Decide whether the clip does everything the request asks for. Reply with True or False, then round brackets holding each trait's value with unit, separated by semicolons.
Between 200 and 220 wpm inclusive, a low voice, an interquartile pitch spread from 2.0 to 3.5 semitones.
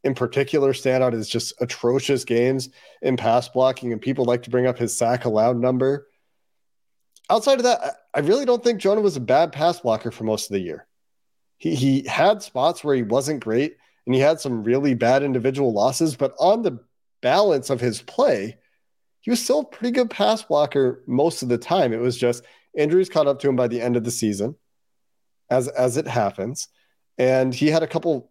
False (205 wpm; 130 Hz; 4.1 semitones)